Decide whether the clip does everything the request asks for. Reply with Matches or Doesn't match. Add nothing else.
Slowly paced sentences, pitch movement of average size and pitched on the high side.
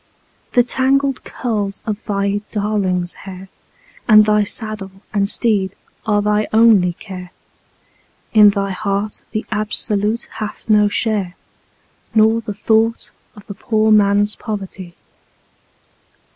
Doesn't match